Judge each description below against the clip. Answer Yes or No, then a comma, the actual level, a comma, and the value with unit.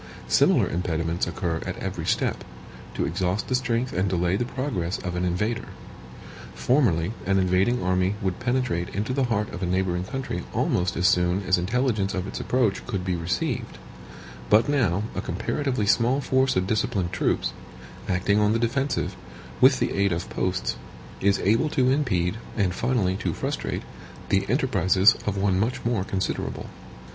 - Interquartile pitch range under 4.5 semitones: No, average, 4.9 semitones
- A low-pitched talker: Yes, very low, 95 Hz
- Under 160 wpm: No, average, 165 wpm